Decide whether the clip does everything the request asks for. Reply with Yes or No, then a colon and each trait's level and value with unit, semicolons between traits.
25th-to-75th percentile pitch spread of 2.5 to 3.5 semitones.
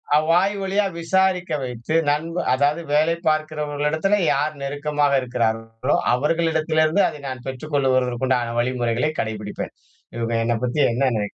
No: average, 4.3 semitones